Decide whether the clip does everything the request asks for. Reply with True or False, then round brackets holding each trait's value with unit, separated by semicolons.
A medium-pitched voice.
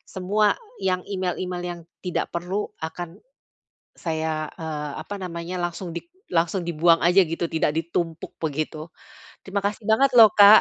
True (175 Hz)